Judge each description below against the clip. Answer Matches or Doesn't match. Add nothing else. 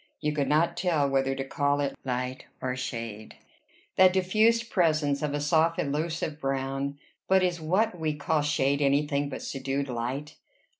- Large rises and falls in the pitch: Doesn't match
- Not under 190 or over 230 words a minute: Doesn't match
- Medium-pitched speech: Matches